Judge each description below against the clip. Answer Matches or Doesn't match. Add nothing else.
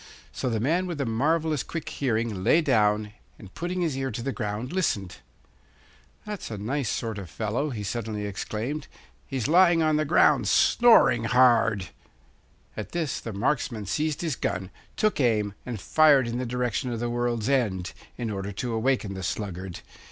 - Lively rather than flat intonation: Matches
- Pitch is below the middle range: Matches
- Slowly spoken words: Doesn't match